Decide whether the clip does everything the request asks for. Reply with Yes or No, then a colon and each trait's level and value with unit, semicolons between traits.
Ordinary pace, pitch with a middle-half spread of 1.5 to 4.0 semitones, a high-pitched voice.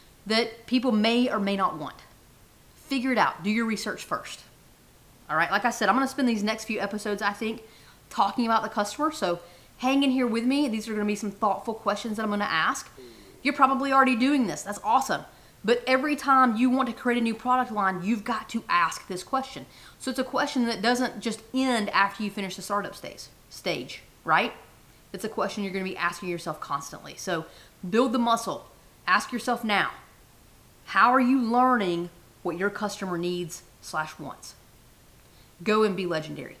No: average, 195 wpm; average, 4.5 semitones; high, 220 Hz